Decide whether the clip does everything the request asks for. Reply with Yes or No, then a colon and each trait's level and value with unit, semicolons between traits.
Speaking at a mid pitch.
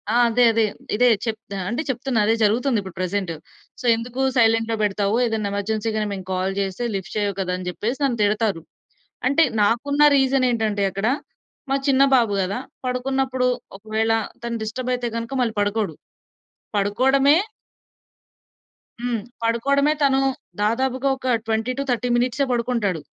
No: high, 230 Hz